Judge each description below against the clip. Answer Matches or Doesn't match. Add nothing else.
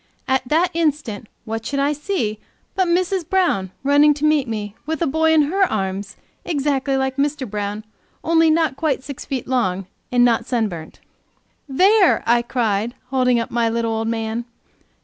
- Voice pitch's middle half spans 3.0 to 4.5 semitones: Doesn't match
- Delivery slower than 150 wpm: Doesn't match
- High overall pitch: Matches